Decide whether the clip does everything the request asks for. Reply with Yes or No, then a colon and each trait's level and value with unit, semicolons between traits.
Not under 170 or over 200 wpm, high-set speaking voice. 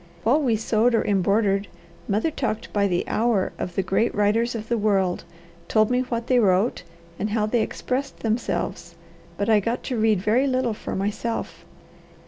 Yes: average, 175 wpm; high, 220 Hz